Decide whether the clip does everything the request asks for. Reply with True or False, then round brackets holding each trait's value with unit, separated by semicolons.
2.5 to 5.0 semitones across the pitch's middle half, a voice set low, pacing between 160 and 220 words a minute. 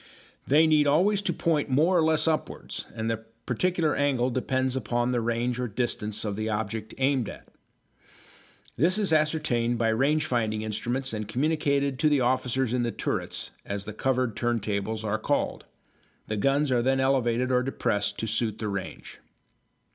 True (4.3 semitones; 125 Hz; 170 wpm)